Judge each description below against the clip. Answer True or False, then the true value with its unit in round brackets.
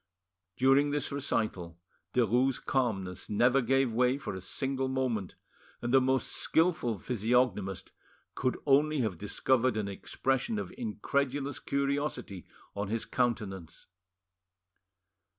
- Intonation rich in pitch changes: False (4.2 semitones)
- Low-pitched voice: True (125 Hz)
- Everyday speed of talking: False (115 wpm)